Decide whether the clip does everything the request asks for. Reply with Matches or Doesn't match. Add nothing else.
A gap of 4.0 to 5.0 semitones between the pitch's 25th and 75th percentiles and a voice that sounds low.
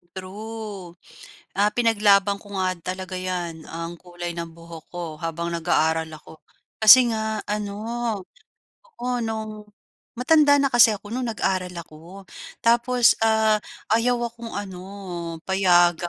Doesn't match